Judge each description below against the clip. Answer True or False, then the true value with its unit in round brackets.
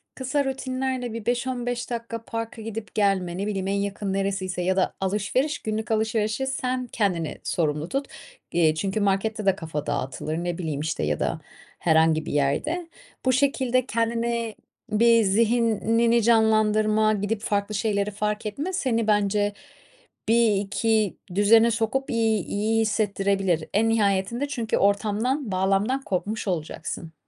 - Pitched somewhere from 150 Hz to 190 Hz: False (215 Hz)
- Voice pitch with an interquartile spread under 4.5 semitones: True (3.1 semitones)